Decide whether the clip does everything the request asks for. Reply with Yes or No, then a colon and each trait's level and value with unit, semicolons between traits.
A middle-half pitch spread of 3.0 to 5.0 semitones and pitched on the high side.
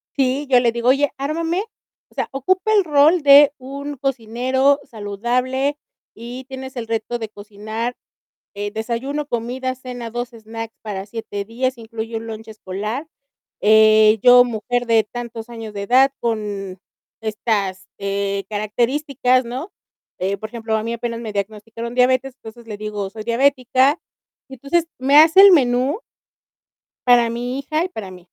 Yes: average, 3.4 semitones; high, 235 Hz